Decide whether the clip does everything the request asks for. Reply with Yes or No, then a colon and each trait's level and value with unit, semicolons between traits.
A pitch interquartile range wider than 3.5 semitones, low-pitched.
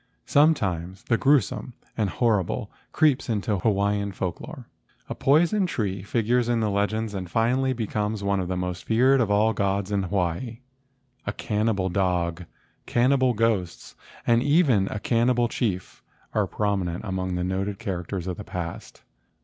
Yes: average, 4.1 semitones; low, 105 Hz